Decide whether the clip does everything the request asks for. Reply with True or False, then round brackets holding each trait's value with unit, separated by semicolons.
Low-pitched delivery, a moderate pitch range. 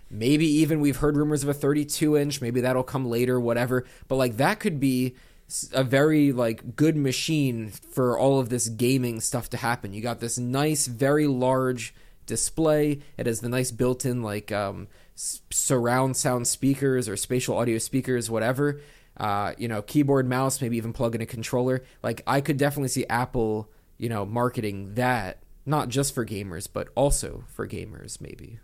True (125 Hz; 3.1 semitones)